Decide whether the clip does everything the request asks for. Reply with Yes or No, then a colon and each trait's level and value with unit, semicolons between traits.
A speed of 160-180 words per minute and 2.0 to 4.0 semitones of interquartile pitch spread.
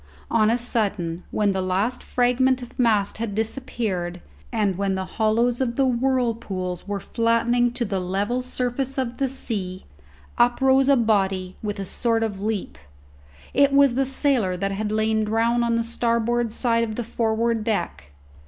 Yes: average, 170 wpm; average, 3.4 semitones